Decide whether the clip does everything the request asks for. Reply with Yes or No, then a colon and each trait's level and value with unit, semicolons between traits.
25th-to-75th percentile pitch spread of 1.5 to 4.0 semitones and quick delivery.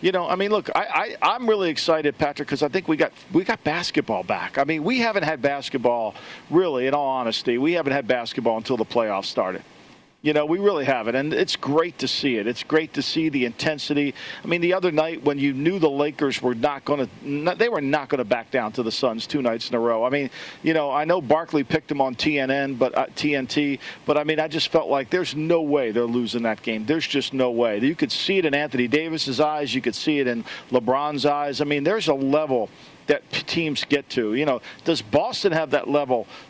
Yes: average, 3.4 semitones; fast, 245 wpm